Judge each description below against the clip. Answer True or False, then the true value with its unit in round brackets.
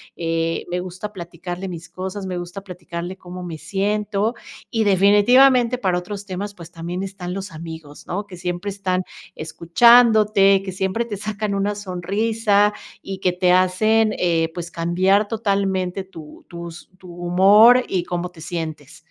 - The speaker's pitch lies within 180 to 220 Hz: True (185 Hz)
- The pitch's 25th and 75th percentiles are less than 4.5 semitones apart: True (2.8 semitones)